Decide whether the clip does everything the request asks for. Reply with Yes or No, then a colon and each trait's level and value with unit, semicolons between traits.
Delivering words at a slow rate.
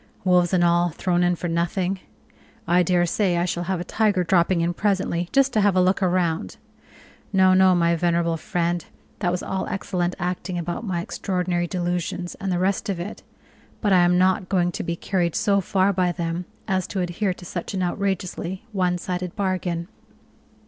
No: average, 185 wpm